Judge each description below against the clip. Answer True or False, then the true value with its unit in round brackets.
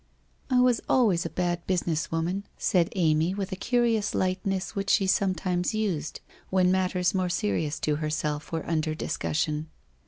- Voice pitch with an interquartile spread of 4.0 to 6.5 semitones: False (3.5 semitones)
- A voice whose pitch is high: False (180 Hz)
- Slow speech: False (165 wpm)